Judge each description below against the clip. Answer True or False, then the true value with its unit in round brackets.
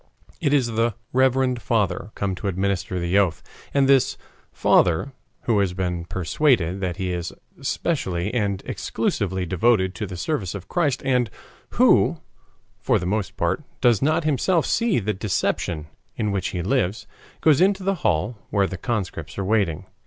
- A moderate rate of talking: True (160 wpm)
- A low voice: True (100 Hz)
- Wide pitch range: True (5.8 semitones)